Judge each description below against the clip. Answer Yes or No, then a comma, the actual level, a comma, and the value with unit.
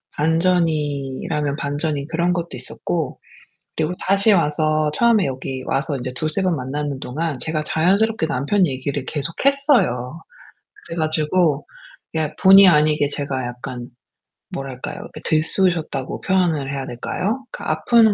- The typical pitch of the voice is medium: Yes, medium, 155 Hz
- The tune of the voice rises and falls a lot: No, average, 4.2 semitones